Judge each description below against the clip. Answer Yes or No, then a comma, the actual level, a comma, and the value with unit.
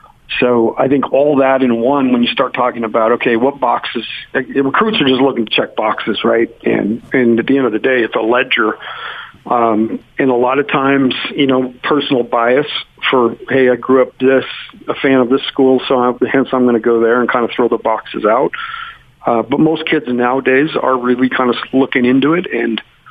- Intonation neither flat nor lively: No, narrow, 1.9 semitones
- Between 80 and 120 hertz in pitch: No, low, 130 Hz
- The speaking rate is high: Yes, fast, 215 wpm